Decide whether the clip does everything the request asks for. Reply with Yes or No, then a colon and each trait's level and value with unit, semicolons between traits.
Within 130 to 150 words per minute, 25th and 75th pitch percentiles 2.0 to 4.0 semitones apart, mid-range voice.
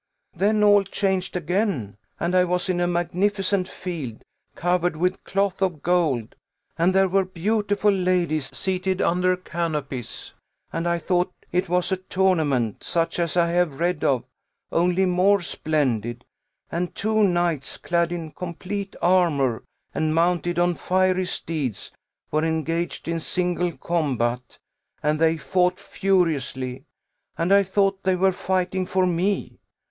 Yes: average, 140 wpm; narrow, 2.6 semitones; medium, 175 Hz